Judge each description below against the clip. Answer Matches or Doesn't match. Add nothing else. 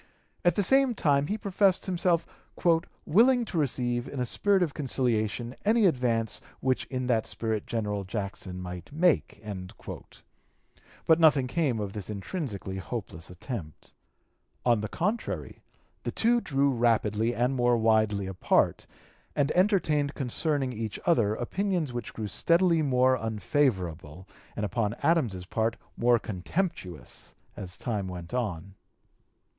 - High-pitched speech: Doesn't match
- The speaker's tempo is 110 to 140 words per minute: Matches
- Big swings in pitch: Matches